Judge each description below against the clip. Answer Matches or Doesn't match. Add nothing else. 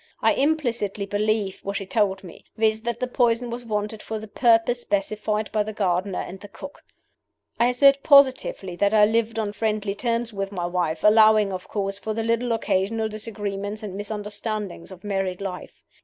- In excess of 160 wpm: Matches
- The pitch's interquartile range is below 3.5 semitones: Matches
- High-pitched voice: Matches